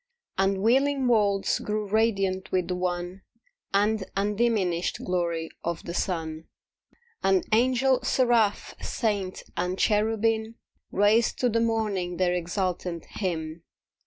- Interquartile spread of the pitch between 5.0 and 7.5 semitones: No, average, 3.8 semitones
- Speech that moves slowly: Yes, slow, 115 wpm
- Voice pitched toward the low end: No, high, 195 Hz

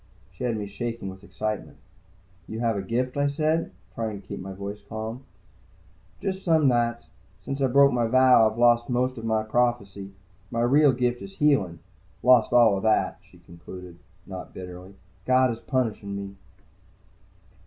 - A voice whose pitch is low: Yes, low, 115 Hz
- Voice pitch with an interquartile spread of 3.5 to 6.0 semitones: Yes, average, 4.1 semitones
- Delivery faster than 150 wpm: Yes, average, 165 wpm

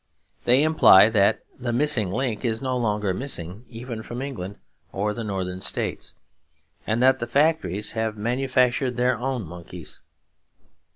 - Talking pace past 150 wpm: No, average, 140 wpm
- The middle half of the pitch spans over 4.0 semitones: No, average, 3.7 semitones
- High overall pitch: No, low, 115 Hz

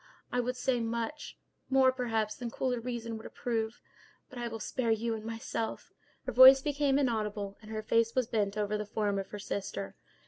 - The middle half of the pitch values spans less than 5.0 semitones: Yes, average, 2.7 semitones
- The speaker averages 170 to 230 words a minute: Yes, average, 185 wpm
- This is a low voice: No, high, 230 Hz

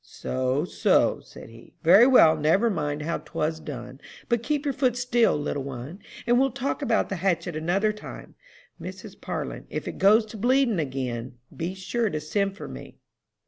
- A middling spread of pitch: No, wide, 7.9 semitones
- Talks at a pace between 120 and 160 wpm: No, average, 180 wpm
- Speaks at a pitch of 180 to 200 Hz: Yes, medium, 185 Hz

